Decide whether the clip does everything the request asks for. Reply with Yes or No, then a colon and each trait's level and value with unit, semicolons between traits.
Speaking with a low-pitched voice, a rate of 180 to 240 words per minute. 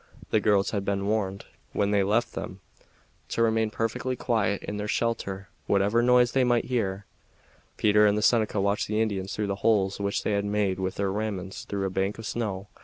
Yes: low, 105 Hz; average, 195 wpm